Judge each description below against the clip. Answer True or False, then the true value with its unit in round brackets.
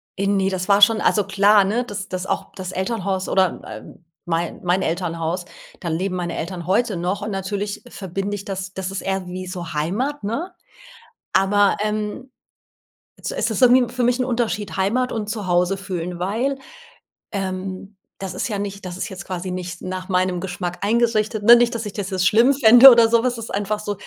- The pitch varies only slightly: False (3.0 semitones)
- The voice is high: True (195 Hz)